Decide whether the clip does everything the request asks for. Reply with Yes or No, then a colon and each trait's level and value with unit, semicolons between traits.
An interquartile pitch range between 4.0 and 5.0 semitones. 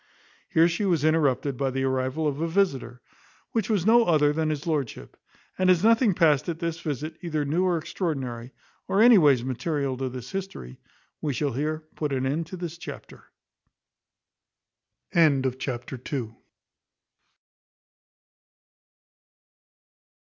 Yes: average, 4.3 semitones